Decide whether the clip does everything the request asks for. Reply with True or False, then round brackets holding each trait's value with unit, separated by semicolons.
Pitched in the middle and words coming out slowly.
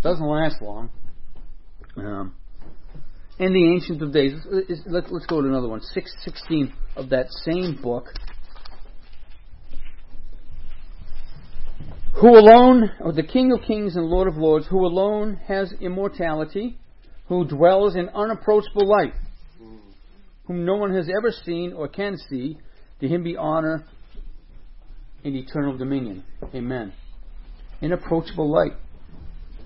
True (155 Hz; 120 wpm)